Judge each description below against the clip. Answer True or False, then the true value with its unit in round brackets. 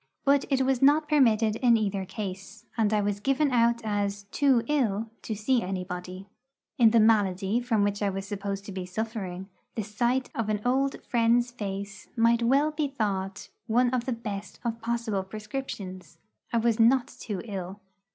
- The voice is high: True (220 Hz)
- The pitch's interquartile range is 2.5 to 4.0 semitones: True (3.5 semitones)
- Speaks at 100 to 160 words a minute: False (175 wpm)